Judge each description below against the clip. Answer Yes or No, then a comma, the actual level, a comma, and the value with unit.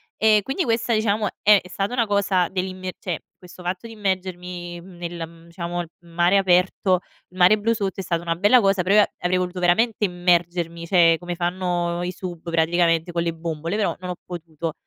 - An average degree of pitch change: No, narrow, 2.3 semitones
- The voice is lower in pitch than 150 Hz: No, medium, 180 Hz